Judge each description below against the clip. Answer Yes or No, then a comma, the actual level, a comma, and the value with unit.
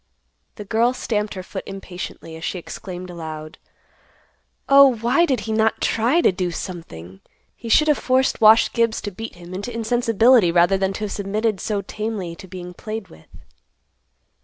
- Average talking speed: Yes, average, 170 wpm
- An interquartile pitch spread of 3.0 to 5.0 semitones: Yes, average, 4.2 semitones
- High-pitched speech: Yes, high, 210 Hz